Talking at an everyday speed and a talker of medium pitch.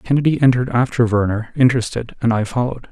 No: average, 165 wpm; low, 120 Hz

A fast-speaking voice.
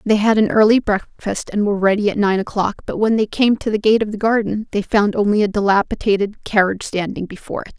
Yes: fast, 230 wpm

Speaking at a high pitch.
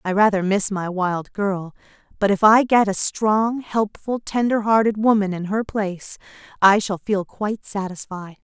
Yes: high, 205 Hz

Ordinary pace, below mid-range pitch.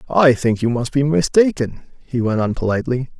Yes: average, 190 wpm; low, 130 Hz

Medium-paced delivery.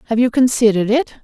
Yes: average, 195 wpm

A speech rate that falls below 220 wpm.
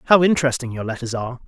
Yes: fast, 205 wpm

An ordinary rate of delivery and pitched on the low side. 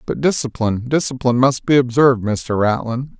Yes: average, 150 wpm; low, 125 Hz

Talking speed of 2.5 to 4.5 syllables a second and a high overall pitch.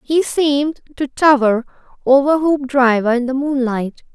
Yes: 4.3 syllables/s; very high, 270 Hz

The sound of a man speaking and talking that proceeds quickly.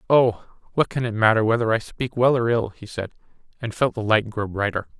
Yes: male; fast, 230 wpm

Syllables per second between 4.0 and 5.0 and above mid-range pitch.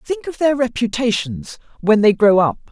Yes: 4.8 syllables/s; high, 235 Hz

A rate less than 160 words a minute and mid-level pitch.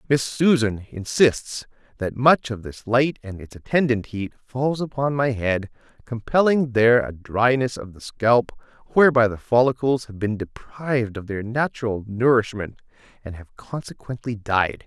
No: average, 150 wpm; low, 120 Hz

